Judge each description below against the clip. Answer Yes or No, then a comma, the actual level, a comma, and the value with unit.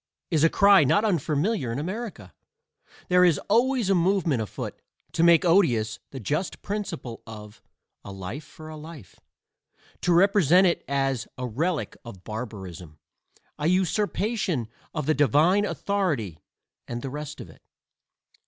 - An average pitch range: No, wide, 7.9 semitones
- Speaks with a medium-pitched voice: Yes, medium, 155 Hz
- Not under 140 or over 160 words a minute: Yes, average, 145 wpm